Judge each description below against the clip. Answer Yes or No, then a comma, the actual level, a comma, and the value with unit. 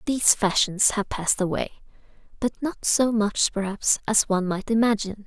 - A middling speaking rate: Yes, average, 160 wpm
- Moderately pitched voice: No, high, 210 Hz